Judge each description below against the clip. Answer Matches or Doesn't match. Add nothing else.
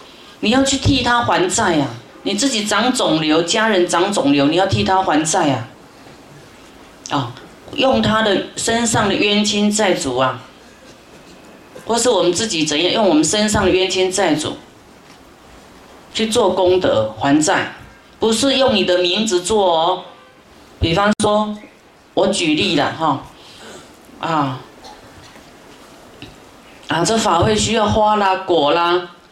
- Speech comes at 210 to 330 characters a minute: Doesn't match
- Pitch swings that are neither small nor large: Matches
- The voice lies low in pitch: Doesn't match